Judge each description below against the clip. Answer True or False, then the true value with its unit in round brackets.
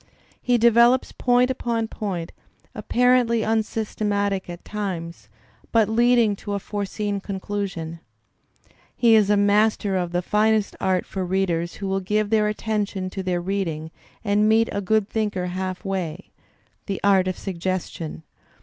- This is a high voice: True (200 Hz)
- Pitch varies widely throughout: False (2.8 semitones)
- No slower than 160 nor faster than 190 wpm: False (140 wpm)